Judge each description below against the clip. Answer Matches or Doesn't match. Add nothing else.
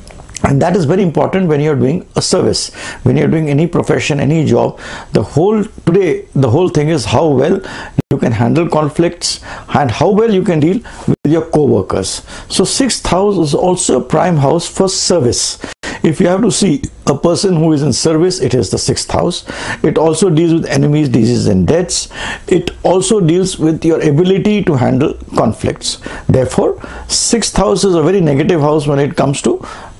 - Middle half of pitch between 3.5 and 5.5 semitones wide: Matches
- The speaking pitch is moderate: Matches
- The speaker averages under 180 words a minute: Doesn't match